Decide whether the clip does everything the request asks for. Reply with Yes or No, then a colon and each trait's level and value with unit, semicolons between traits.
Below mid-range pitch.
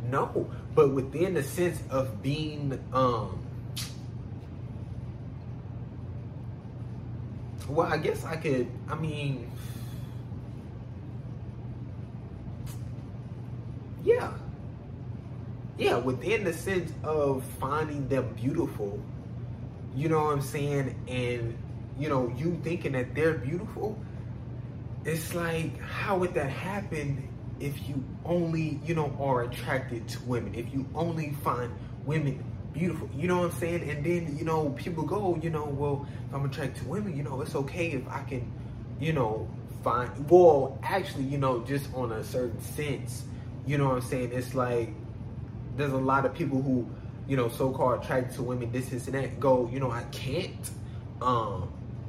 Yes: low, 125 Hz